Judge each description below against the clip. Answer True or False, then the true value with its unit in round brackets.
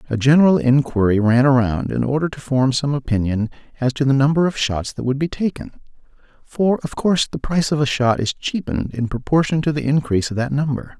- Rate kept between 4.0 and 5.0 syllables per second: False (6.0 syllables/s)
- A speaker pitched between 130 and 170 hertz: True (135 Hz)